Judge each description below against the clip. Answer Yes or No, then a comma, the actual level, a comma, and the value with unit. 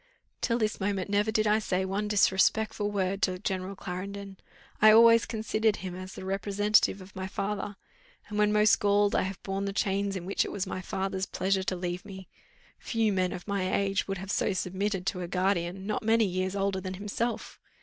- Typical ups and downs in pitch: No, narrow, 1.8 semitones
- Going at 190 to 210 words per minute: Yes, average, 200 wpm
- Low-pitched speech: No, high, 195 Hz